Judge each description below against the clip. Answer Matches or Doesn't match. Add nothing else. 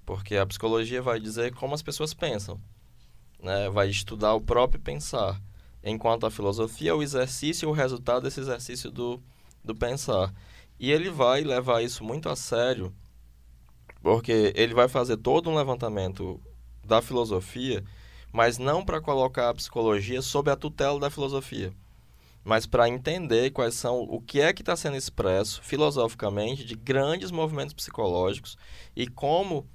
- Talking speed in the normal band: Matches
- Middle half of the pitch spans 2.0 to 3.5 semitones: Doesn't match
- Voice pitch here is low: Matches